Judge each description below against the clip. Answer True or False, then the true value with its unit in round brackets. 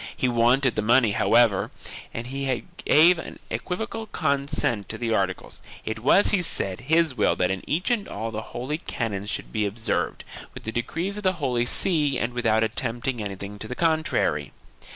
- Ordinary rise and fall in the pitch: False (6.0 semitones)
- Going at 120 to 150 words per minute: False (180 wpm)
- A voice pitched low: True (120 Hz)